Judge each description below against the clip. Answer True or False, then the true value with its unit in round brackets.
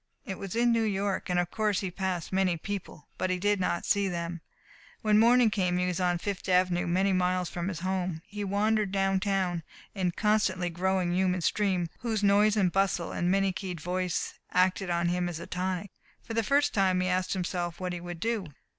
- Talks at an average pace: False (210 wpm)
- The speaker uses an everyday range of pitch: False (2.1 semitones)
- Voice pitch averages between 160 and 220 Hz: True (185 Hz)